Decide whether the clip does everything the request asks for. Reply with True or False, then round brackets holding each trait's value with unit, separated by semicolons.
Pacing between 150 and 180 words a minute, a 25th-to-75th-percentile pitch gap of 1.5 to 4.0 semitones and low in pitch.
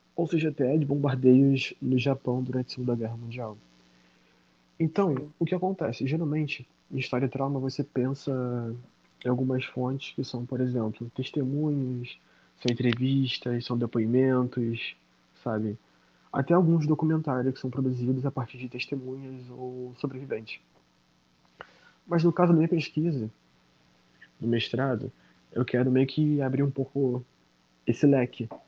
False (135 wpm; 2.8 semitones; 130 Hz)